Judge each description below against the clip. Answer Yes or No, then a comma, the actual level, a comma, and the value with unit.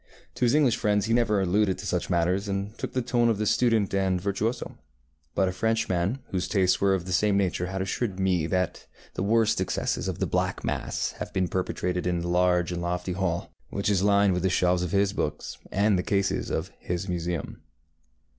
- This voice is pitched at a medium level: No, very low, 95 Hz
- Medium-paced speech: No, fast, 210 wpm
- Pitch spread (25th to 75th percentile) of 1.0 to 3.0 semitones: Yes, narrow, 2.4 semitones